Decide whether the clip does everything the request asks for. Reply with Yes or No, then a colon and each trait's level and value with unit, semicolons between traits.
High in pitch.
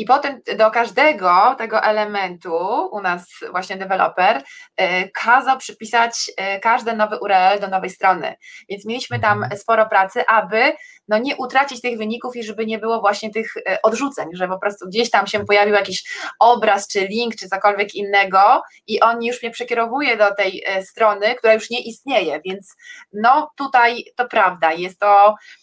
Yes: high, 220 Hz